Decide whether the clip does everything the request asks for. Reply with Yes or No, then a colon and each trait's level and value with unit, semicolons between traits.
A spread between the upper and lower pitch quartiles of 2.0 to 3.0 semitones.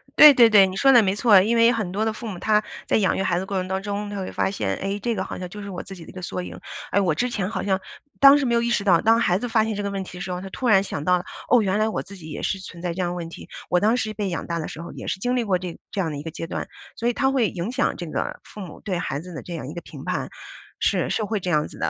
No: average, 3.7 semitones